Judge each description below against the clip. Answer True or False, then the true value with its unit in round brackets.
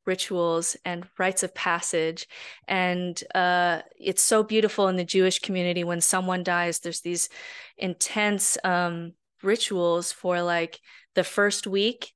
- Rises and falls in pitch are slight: True (2.1 semitones)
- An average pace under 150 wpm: True (135 wpm)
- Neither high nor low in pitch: True (180 Hz)